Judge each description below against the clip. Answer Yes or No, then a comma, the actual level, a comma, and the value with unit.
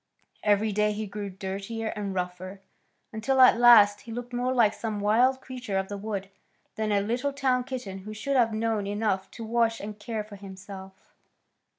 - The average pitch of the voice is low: No, high, 215 Hz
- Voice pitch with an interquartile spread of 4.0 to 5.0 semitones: No, average, 2.9 semitones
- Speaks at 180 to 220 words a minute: Yes, average, 185 wpm